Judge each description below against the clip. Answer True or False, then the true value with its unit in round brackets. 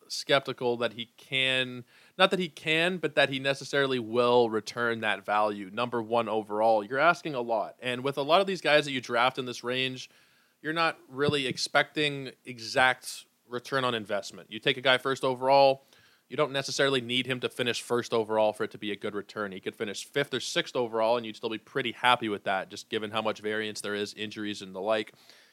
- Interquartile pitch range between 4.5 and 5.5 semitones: False (3.6 semitones)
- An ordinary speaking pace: False (215 wpm)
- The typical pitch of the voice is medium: False (125 Hz)